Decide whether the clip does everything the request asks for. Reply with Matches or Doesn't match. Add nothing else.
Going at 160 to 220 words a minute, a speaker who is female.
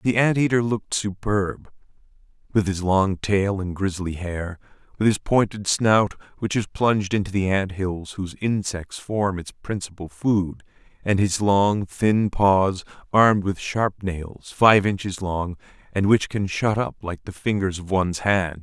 Doesn't match